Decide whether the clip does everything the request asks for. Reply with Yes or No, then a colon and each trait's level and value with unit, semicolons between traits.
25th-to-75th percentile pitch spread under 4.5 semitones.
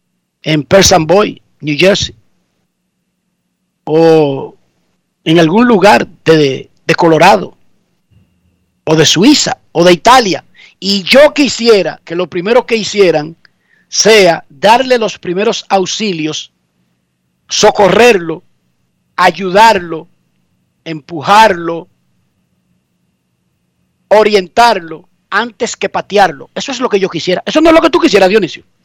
No: wide, 5.6 semitones